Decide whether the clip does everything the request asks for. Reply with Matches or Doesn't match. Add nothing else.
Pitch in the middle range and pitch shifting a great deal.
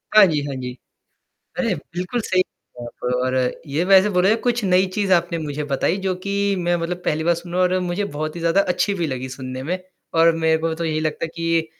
Doesn't match